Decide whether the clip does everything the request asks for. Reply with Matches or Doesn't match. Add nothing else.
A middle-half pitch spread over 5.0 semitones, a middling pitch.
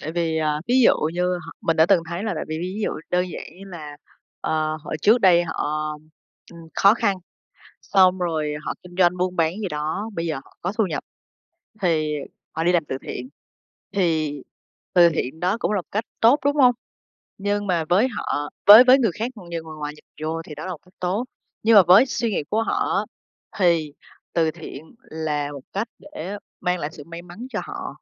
Doesn't match